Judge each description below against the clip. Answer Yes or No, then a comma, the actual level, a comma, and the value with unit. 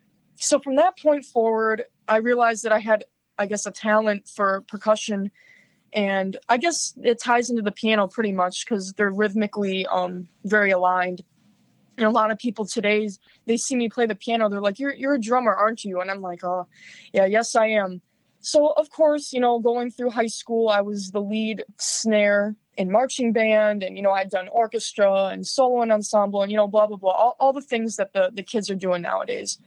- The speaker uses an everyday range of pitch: Yes, average, 3.0 semitones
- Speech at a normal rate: No, fast, 210 wpm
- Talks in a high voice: Yes, high, 215 Hz